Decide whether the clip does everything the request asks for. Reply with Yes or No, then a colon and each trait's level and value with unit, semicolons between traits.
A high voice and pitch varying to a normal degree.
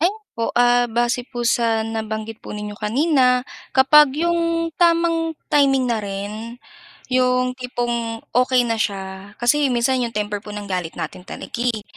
Yes: high, 240 Hz; average, 3.4 semitones